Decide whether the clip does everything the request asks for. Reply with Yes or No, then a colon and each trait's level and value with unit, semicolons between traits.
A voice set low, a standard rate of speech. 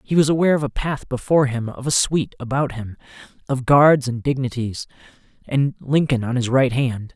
Yes: low, 130 Hz; average, 195 wpm